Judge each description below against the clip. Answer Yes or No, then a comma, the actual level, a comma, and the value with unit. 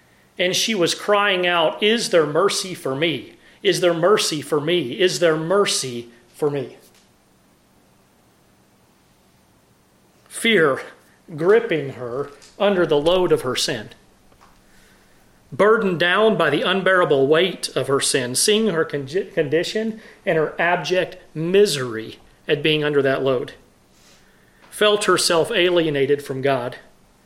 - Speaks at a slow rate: Yes, slow, 125 wpm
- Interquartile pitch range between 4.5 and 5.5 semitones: Yes, average, 5.1 semitones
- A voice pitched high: No, medium, 175 Hz